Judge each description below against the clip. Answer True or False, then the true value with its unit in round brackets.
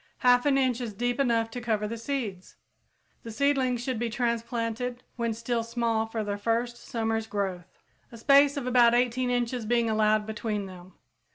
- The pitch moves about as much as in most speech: False (2.0 semitones)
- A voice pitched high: True (235 Hz)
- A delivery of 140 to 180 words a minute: True (175 wpm)